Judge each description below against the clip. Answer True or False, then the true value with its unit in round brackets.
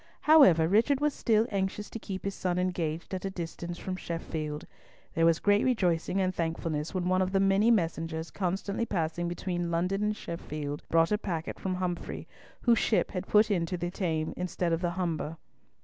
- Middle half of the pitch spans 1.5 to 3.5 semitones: True (2.9 semitones)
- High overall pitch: False (180 Hz)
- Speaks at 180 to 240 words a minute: True (185 wpm)